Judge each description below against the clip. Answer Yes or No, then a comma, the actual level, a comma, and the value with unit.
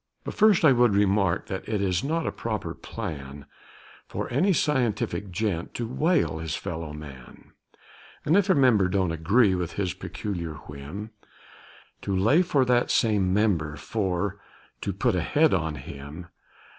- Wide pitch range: Yes, wide, 6.7 semitones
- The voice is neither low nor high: No, low, 100 Hz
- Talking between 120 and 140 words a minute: No, average, 155 wpm